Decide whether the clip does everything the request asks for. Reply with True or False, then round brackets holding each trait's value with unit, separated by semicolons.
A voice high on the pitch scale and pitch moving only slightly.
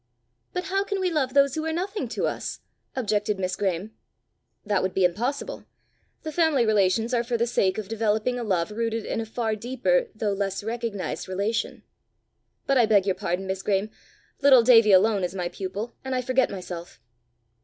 False (220 Hz; 4.8 semitones)